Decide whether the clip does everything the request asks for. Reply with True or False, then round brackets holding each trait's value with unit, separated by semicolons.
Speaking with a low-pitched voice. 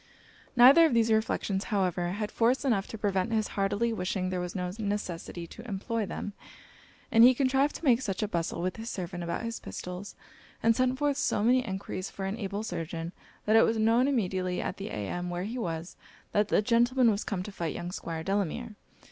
False (205 Hz)